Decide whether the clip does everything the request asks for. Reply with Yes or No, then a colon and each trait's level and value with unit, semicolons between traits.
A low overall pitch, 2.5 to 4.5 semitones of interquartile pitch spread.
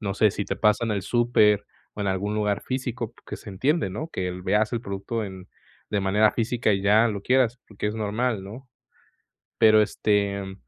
Yes: low, 105 Hz; average, 2.8 semitones